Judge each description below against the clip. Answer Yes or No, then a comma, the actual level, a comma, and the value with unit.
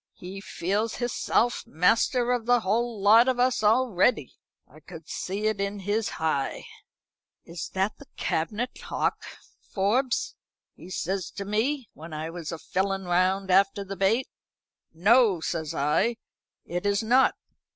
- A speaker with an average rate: Yes, average, 145 wpm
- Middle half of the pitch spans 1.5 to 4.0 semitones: No, average, 4.5 semitones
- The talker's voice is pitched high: Yes, high, 200 Hz